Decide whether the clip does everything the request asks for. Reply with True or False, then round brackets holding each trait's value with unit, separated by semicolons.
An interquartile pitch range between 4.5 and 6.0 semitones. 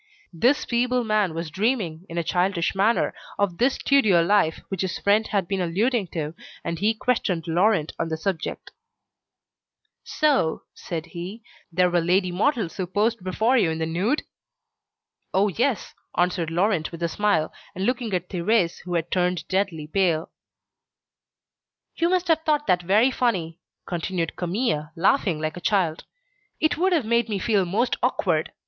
True (5.0 semitones)